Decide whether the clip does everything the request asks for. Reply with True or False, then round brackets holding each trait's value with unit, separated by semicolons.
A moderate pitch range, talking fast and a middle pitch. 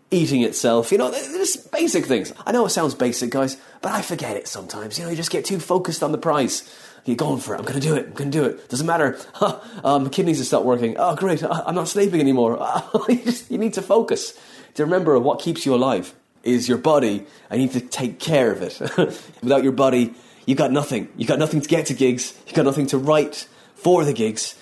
False (6.2 semitones; 245 wpm; 150 Hz)